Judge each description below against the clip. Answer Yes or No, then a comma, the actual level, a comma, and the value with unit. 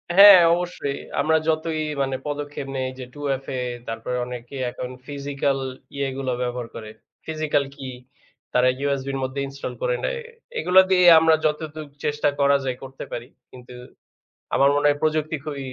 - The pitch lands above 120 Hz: Yes, medium, 140 Hz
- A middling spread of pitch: Yes, average, 3.0 semitones